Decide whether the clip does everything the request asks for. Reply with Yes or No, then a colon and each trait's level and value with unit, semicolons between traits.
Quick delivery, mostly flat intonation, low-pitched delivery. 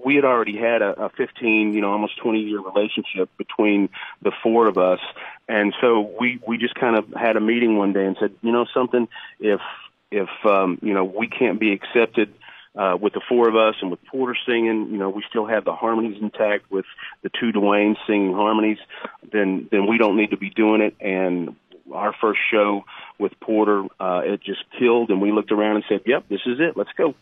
Yes: fast, 215 wpm; narrow, 2.3 semitones; low, 105 Hz